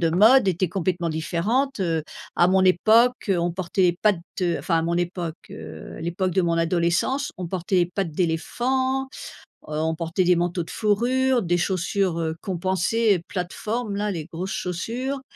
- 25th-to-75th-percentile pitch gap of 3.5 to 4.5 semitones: Yes, average, 3.8 semitones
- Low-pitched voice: No, medium, 180 Hz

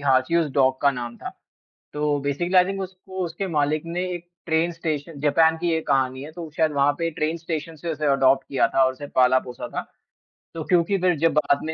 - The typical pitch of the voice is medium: Yes, medium, 155 Hz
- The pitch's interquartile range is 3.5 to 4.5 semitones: No, average, 3.1 semitones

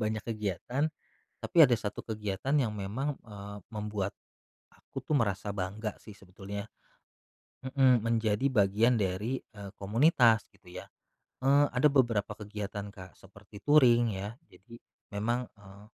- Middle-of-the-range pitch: No, low, 110 Hz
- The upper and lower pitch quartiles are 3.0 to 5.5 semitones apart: Yes, average, 3.3 semitones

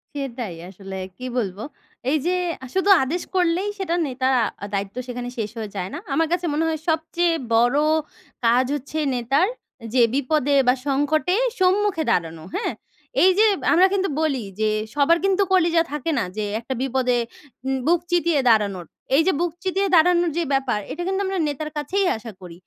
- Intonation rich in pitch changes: Yes, wide, 6.3 semitones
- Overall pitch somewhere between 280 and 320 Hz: Yes, very high, 290 Hz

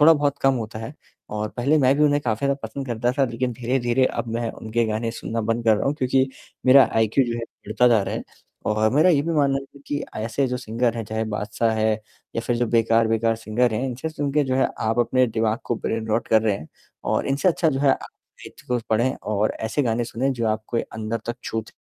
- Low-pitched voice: Yes, low, 120 Hz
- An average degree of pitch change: Yes, average, 3.2 semitones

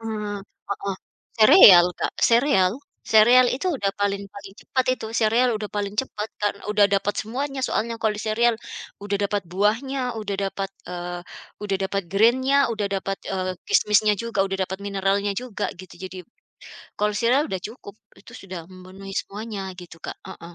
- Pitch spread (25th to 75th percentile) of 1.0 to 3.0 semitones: Yes, narrow, 2.6 semitones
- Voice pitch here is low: No, high, 205 Hz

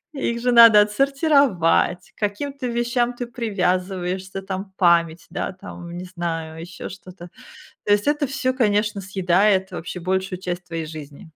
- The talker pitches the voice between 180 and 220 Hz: Yes, high, 190 Hz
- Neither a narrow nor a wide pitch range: Yes, average, 4.8 semitones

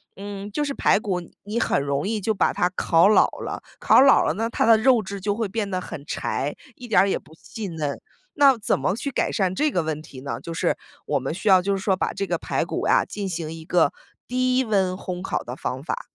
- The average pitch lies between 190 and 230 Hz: Yes, high, 195 Hz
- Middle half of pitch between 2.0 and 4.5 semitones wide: No, average, 5.0 semitones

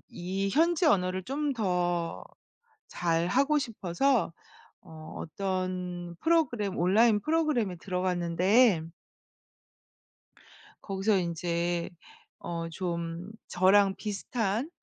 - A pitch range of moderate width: Yes, average, 4.6 semitones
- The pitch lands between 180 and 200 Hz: Yes, medium, 185 Hz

